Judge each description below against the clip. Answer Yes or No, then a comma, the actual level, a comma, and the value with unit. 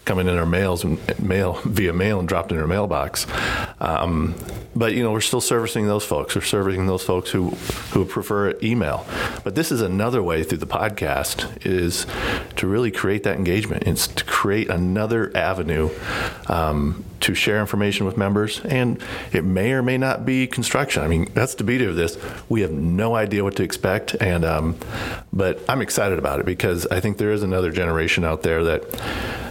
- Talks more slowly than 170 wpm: No, average, 190 wpm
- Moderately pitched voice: No, very low, 95 Hz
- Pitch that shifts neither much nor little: Yes, average, 3.9 semitones